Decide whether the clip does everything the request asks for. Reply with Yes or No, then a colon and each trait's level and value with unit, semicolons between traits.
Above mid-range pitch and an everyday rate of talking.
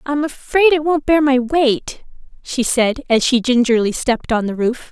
Yes: very high, 260 Hz; average, 195 wpm